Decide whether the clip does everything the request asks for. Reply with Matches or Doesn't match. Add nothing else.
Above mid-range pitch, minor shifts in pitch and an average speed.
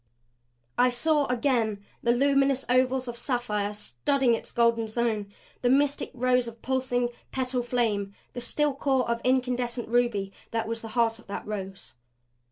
Matches